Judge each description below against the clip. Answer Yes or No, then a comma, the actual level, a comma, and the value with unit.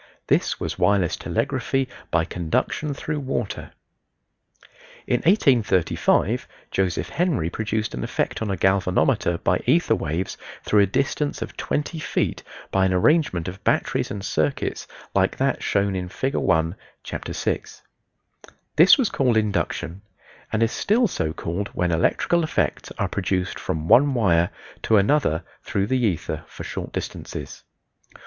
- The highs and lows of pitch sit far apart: Yes, wide, 7.2 semitones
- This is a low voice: Yes, low, 100 Hz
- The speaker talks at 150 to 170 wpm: No, average, 140 wpm